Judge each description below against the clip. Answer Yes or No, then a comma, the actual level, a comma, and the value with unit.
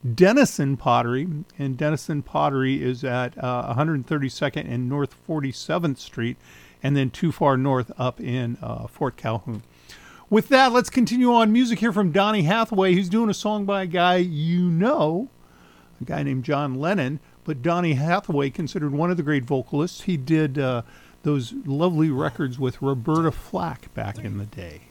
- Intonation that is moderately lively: No, wide, 5.7 semitones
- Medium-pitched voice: Yes, medium, 145 Hz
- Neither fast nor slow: Yes, average, 165 wpm